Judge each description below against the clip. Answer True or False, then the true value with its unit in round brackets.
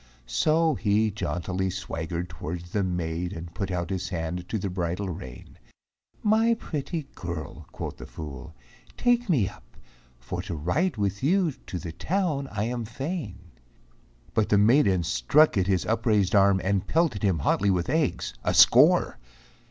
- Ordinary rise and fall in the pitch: False (7.2 semitones)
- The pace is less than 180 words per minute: True (160 wpm)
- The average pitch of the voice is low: True (100 Hz)